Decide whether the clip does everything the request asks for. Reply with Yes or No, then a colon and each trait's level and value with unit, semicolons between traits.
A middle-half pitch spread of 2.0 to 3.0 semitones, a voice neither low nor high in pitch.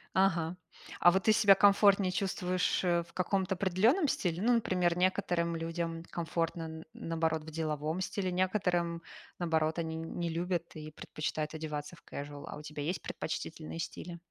Yes: narrow, 2.6 semitones; medium, 170 Hz